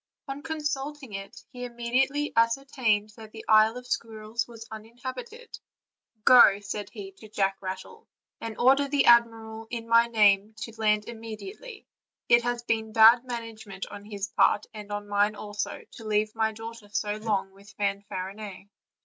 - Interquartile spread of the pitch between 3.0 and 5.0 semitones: No, narrow, 2.6 semitones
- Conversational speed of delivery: Yes, average, 155 wpm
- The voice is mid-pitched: No, high, 220 Hz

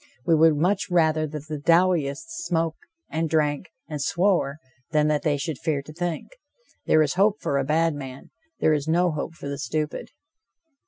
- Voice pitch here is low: No, medium, 155 Hz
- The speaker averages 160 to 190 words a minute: Yes, average, 180 wpm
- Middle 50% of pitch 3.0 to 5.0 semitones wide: No, narrow, 2.4 semitones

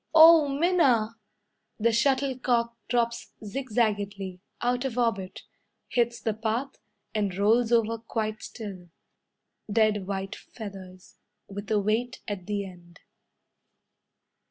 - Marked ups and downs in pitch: No, average, 3.3 semitones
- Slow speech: Yes, slow, 110 wpm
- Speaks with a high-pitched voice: Yes, high, 220 Hz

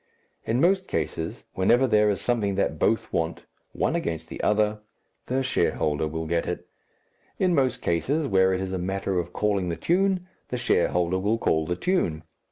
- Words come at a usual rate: Yes, average, 175 wpm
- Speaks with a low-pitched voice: Yes, low, 100 Hz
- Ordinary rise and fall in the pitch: No, wide, 6.2 semitones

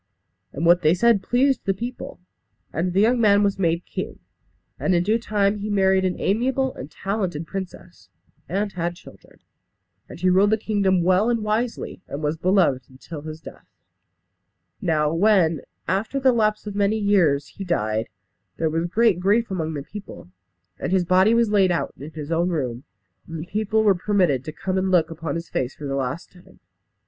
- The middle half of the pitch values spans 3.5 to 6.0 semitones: Yes, average, 4.3 semitones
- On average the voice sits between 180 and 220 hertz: Yes, medium, 185 Hz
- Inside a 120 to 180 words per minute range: No, average, 190 wpm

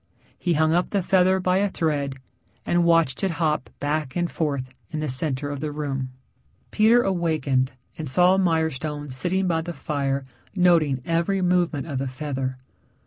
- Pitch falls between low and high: Yes, medium, 155 Hz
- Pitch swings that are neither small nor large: Yes, average, 4.1 semitones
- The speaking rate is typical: Yes, average, 165 wpm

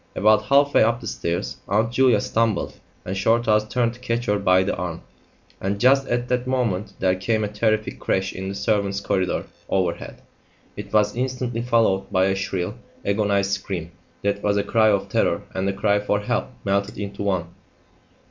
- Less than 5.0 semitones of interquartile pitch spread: Yes, average, 3.0 semitones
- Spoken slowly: No, average, 185 wpm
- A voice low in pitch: Yes, low, 105 Hz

